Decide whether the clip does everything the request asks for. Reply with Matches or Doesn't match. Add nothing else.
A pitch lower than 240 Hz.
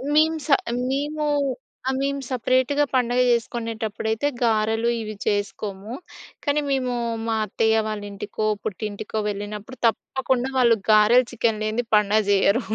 Matches